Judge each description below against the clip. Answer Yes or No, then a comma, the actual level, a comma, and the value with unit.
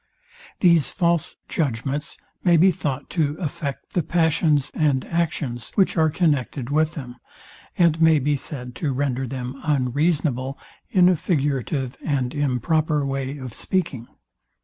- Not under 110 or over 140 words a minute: Yes, slow, 135 wpm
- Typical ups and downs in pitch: Yes, average, 3.5 semitones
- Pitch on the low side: No, medium, 145 Hz